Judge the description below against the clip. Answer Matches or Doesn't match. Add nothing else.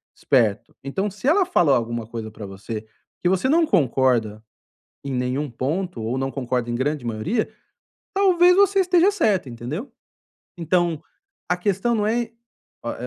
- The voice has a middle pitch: Matches